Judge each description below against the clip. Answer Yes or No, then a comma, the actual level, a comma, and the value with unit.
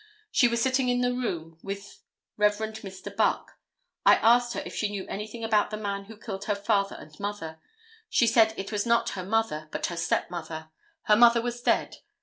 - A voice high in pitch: Yes, high, 210 Hz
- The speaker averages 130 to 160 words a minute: No, average, 200 wpm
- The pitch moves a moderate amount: Yes, average, 3.1 semitones